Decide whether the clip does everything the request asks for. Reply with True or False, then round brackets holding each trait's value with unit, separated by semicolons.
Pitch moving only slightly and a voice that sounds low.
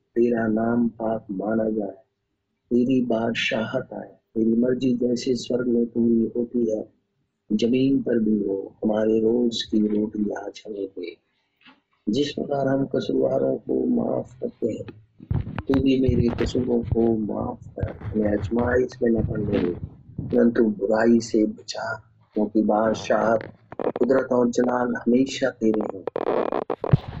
True (2.3 semitones; 115 Hz)